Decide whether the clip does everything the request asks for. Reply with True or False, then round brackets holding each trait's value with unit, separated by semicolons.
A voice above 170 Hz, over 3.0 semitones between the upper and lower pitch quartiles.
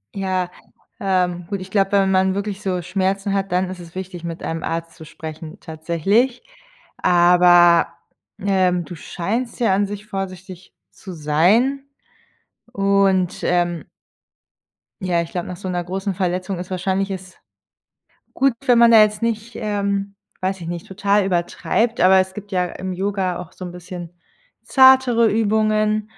False (190 Hz; 2.4 semitones)